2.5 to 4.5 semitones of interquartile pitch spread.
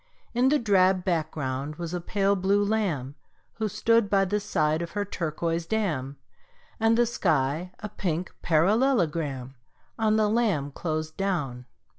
No: average, 5.2 semitones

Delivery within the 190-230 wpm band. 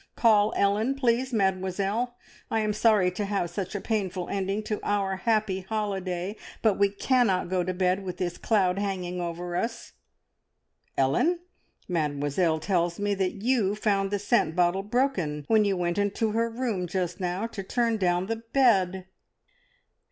No: average, 160 wpm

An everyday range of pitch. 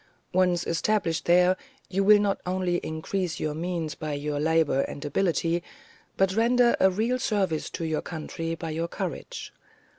Yes: average, 3.3 semitones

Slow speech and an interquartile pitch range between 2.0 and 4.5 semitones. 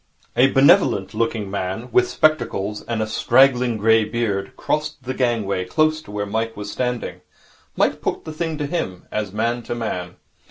No: average, 170 wpm; average, 4.1 semitones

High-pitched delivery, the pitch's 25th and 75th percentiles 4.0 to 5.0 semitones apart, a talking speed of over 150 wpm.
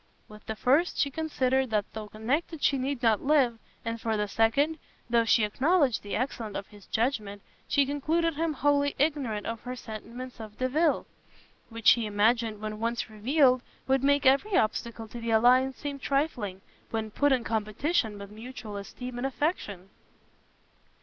Yes: high, 245 Hz; average, 4.4 semitones; average, 165 wpm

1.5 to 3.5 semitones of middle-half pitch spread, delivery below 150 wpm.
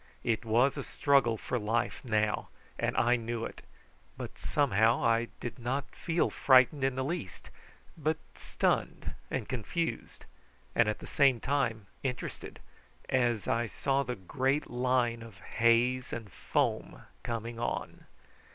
Yes: average, 2.7 semitones; average, 140 wpm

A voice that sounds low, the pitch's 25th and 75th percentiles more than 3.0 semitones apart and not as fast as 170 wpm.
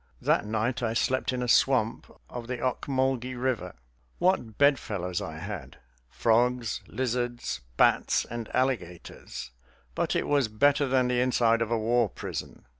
No: low, 120 Hz; average, 2.7 semitones; average, 145 wpm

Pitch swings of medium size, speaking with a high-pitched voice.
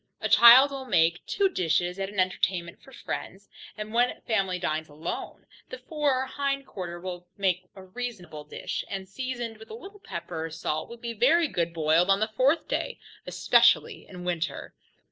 No: wide, 6.6 semitones; high, 195 Hz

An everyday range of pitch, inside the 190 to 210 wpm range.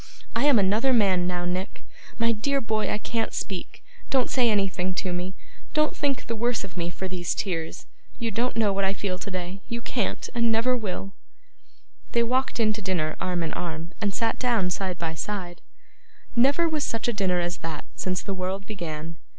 Yes: average, 4.4 semitones; average, 195 wpm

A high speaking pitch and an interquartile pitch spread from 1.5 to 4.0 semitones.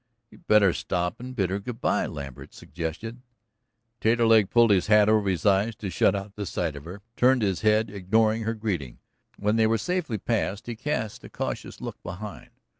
No: low, 105 Hz; average, 3.0 semitones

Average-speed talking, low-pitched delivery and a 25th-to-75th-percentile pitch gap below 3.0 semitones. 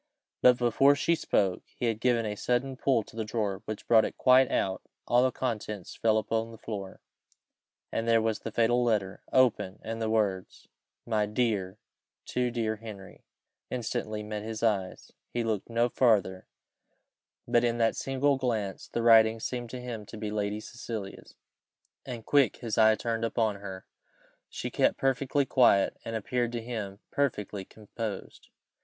Yes: average, 165 wpm; low, 115 Hz; narrow, 2.4 semitones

